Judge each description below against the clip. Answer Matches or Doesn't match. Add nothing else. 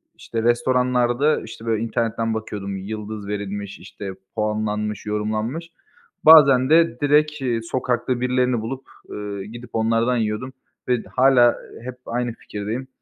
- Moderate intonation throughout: Matches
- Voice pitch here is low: Matches